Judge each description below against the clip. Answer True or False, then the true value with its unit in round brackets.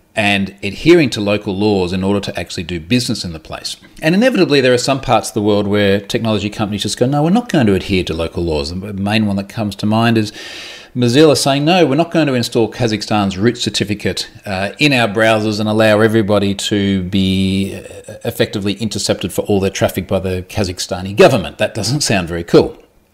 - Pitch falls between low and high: False (105 Hz)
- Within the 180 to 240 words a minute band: True (205 wpm)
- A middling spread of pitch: True (3.3 semitones)